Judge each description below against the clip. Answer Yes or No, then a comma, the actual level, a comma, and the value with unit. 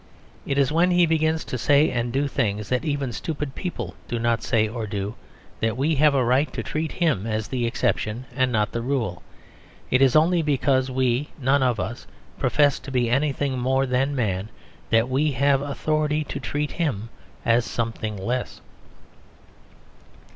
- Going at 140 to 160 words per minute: No, average, 175 wpm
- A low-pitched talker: Yes, low, 130 Hz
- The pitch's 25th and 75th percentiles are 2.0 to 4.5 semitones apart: Yes, average, 3.7 semitones